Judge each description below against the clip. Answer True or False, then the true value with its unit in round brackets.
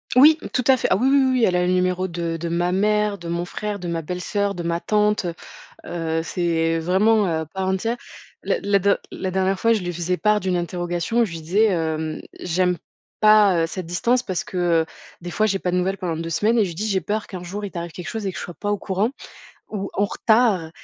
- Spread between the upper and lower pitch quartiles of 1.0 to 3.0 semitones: False (3.4 semitones)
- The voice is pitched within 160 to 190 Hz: True (185 Hz)